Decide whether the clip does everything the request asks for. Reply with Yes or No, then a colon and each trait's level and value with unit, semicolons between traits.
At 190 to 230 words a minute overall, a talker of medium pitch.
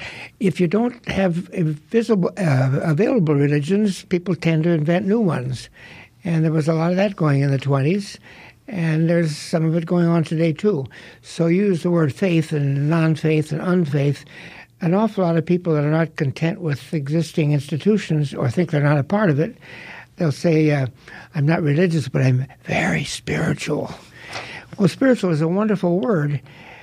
No: average, 180 wpm; medium, 165 Hz